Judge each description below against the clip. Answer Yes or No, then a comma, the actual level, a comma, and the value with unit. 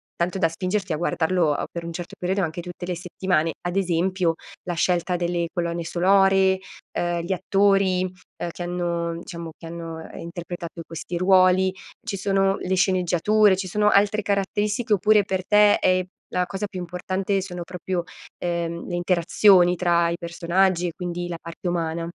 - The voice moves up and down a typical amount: No, narrow, 2.0 semitones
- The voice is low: No, medium, 180 Hz